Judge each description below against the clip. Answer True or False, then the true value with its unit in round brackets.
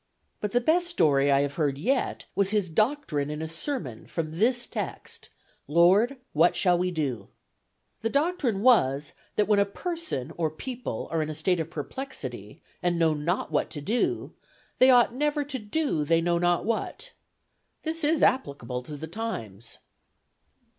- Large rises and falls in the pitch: True (8.7 semitones)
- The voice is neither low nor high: True (175 Hz)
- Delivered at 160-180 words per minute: True (165 wpm)